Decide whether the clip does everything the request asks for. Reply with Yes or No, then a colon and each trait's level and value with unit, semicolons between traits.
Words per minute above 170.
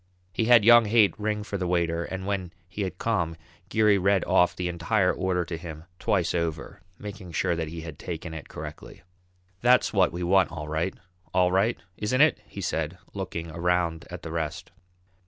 Yes: average, 190 wpm